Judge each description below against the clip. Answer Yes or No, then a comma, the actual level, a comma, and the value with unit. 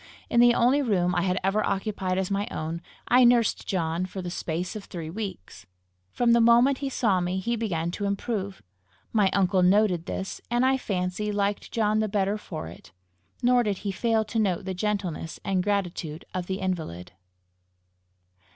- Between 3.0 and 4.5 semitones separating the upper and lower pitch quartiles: Yes, average, 3.3 semitones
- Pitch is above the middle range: Yes, high, 195 Hz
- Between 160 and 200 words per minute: Yes, average, 180 wpm